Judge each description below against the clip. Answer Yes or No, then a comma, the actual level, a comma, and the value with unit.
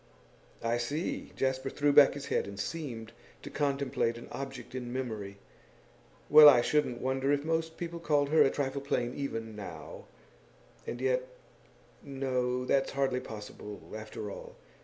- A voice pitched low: Yes, low, 130 Hz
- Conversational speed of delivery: Yes, average, 150 wpm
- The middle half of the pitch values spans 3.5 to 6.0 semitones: No, average, 3.1 semitones